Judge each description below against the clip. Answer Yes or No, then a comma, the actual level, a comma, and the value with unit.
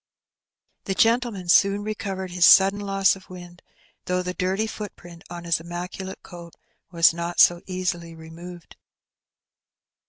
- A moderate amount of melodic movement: No, narrow, 2.1 semitones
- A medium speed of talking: No, slow, 130 wpm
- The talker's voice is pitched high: No, medium, 180 Hz